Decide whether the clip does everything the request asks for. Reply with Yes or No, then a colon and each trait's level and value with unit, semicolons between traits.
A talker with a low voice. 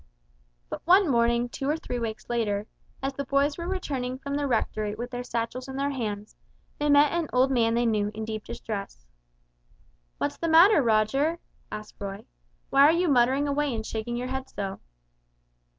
No: very high, 250 Hz